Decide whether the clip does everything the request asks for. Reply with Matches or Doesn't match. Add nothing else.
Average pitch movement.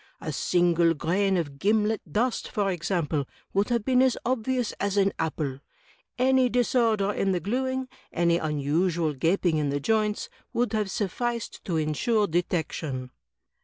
Doesn't match